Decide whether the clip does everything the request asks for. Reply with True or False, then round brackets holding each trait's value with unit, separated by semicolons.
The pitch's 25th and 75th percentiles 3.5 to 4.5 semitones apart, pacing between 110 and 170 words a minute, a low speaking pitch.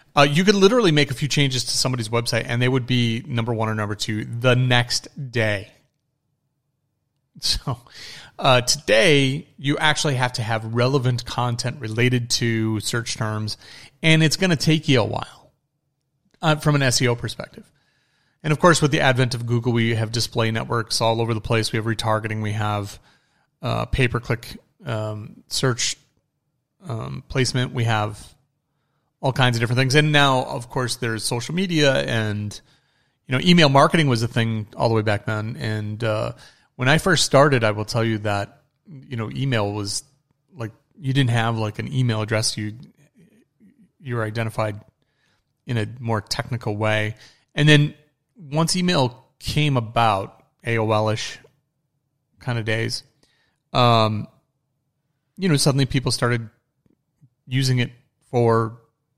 True (4.0 semitones; 160 wpm; 125 Hz)